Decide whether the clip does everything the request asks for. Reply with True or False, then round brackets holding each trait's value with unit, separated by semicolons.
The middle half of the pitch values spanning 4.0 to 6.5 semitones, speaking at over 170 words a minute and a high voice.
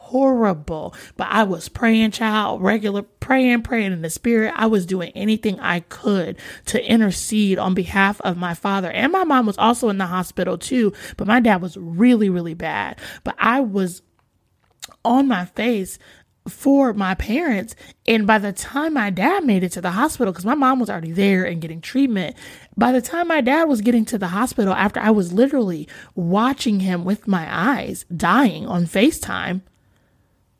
True (4.8 semitones; 180 wpm; 210 Hz)